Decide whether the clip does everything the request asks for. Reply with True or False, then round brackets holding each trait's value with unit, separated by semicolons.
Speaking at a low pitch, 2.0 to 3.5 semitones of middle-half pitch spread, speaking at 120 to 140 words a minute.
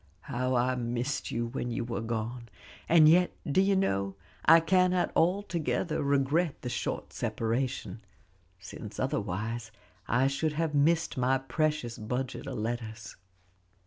False (130 Hz; 5.1 semitones; 135 wpm)